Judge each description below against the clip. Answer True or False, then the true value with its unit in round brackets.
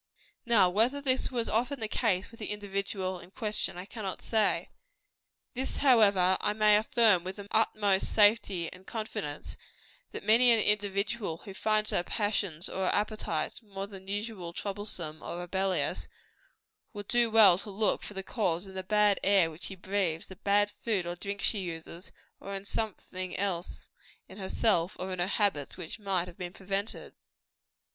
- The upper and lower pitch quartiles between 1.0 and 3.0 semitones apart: True (2.5 semitones)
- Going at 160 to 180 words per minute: True (170 wpm)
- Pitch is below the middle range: False (200 Hz)